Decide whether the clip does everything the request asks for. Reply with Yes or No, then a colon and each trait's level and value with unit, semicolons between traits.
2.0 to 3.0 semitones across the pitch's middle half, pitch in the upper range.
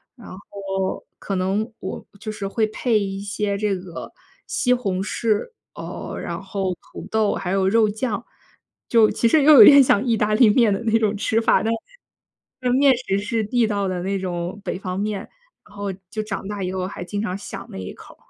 Yes: narrow, 2.6 semitones; high, 205 Hz